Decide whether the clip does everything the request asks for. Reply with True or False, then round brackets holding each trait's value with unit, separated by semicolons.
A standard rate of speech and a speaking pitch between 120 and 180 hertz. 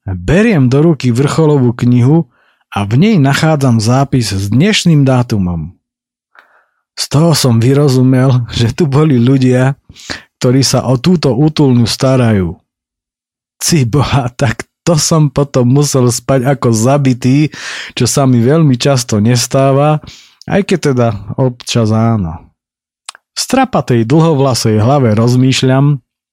True (120 wpm; 130 Hz)